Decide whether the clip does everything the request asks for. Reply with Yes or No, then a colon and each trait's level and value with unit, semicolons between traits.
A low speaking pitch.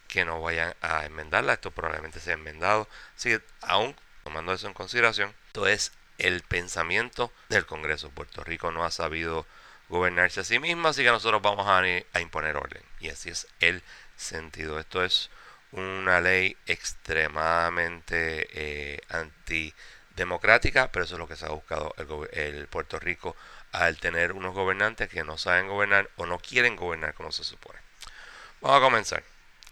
Yes: very low, 85 Hz